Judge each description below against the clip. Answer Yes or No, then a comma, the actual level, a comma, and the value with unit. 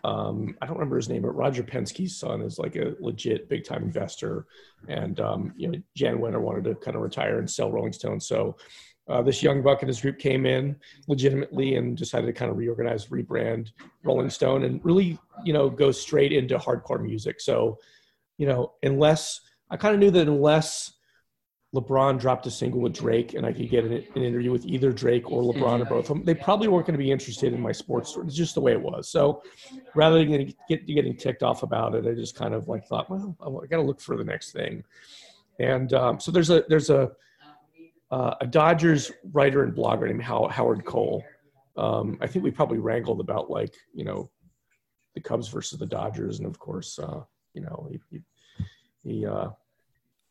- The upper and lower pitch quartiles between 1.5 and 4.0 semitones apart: No, average, 4.5 semitones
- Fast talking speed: Yes, fast, 210 wpm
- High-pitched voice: No, medium, 140 Hz